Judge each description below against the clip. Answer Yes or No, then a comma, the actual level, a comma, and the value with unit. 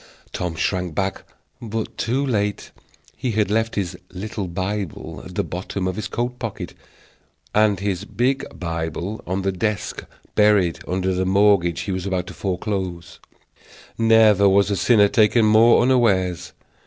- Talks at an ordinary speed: Yes, average, 145 wpm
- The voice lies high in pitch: No, low, 100 Hz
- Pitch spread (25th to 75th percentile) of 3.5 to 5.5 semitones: No, average, 2.9 semitones